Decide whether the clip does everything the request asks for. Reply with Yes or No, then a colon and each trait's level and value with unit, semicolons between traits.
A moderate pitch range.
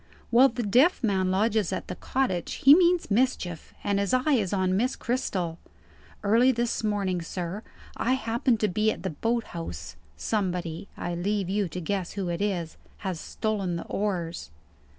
Yes: average, 4.5 semitones